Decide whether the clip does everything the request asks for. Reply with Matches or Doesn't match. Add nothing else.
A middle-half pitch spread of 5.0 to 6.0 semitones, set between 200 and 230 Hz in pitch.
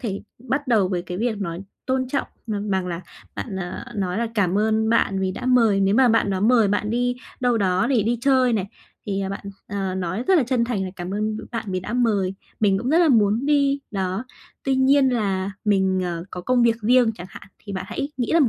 Doesn't match